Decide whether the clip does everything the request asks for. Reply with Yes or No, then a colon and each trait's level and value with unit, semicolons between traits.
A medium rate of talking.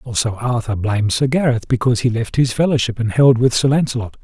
No: fast, 215 wpm